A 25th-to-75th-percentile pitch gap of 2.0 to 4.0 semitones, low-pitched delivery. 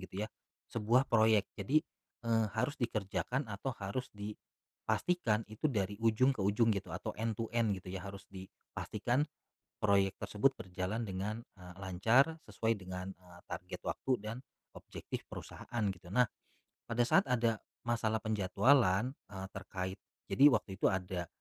Yes: average, 3.5 semitones; low, 105 Hz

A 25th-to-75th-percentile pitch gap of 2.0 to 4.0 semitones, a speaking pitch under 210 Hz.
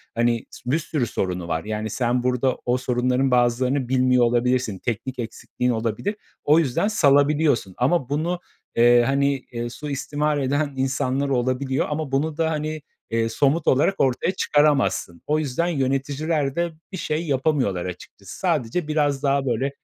Yes: average, 3.6 semitones; low, 135 Hz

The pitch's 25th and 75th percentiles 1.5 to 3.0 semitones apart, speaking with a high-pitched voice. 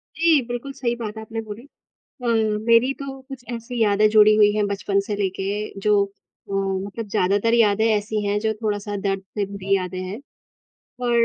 Yes: narrow, 2.5 semitones; high, 210 Hz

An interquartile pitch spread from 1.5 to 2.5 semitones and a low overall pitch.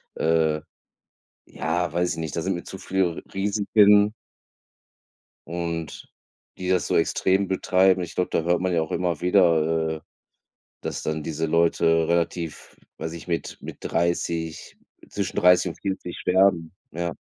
Yes: narrow, 2.1 semitones; very low, 85 Hz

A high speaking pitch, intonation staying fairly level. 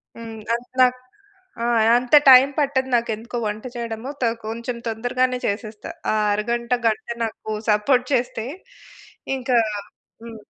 Yes: high, 235 Hz; narrow, 2.2 semitones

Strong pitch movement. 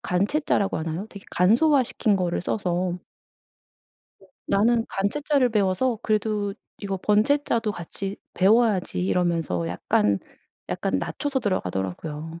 No: average, 4.5 semitones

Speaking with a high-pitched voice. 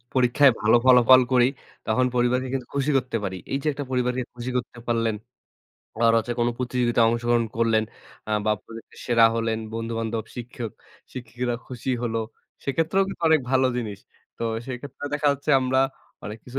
No: low, 120 Hz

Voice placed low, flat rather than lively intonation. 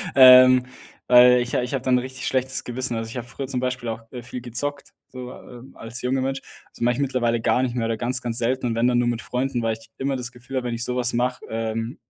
Yes: low, 125 Hz; narrow, 1.4 semitones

